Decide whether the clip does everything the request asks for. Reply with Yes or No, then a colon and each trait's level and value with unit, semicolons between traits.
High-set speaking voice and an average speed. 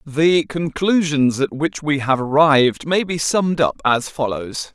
No: medium, 150 Hz; average, 165 wpm